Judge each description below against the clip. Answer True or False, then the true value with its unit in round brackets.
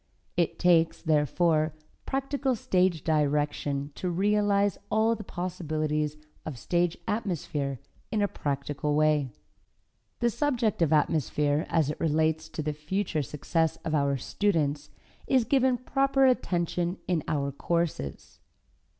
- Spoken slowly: True (125 wpm)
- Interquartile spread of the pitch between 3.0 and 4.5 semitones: False (5.2 semitones)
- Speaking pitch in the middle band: True (165 Hz)